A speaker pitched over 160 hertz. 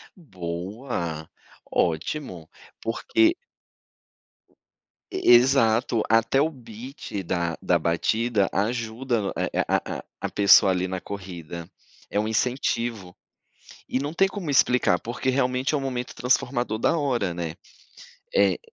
No: low, 115 Hz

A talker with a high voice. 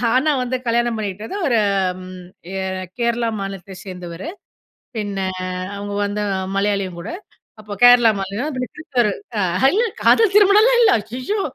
Yes: high, 225 Hz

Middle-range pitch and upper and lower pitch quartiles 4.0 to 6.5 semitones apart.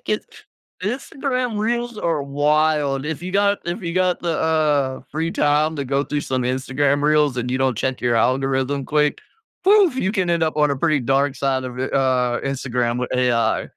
Yes: medium, 145 Hz; average, 4.3 semitones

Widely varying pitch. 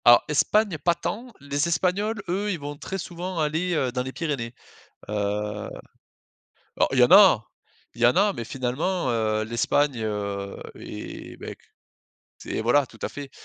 Yes: wide, 7.4 semitones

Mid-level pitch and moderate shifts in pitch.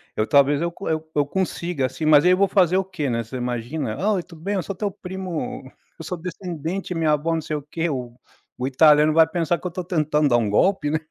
Yes: medium, 160 Hz; average, 4.0 semitones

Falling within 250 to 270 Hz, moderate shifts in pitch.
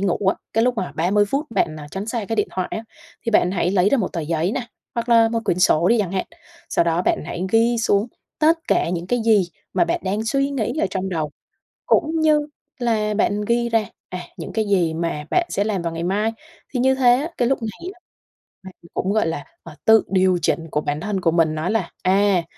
No: high, 205 Hz; average, 4.7 semitones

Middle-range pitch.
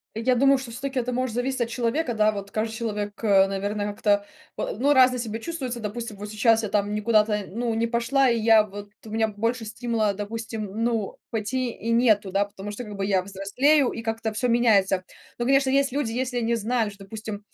No: high, 225 Hz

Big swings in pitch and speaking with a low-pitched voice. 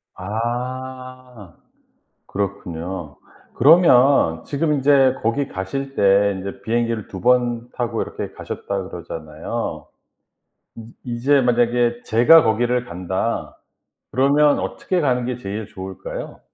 No: average, 4.6 semitones; low, 120 Hz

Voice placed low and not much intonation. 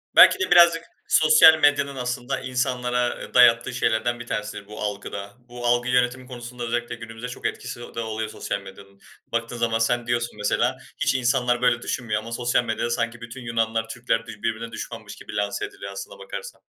Yes: low, 120 Hz; narrow, 1.8 semitones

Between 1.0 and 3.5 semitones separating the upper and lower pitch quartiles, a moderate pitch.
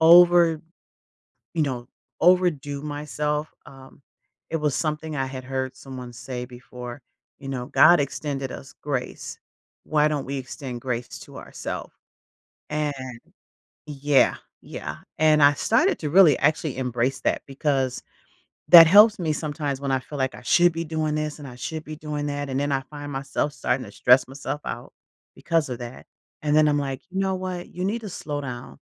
Yes: average, 2.8 semitones; medium, 145 Hz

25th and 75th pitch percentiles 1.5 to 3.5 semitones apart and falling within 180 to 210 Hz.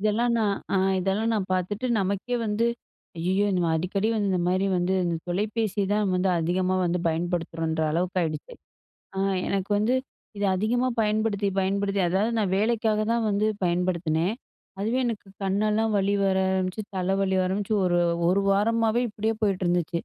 Yes: average, 2.8 semitones; high, 195 Hz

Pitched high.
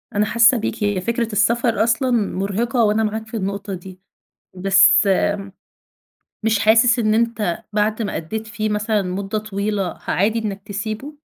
Yes: high, 215 Hz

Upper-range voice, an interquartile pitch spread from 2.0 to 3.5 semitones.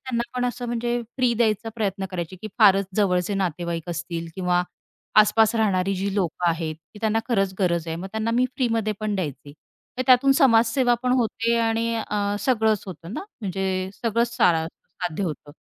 No: high, 205 Hz; average, 4.3 semitones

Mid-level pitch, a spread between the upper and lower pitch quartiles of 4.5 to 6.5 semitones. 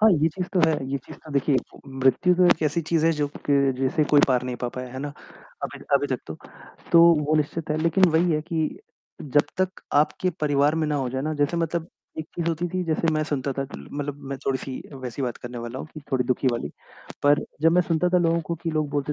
No: medium, 150 Hz; average, 3.4 semitones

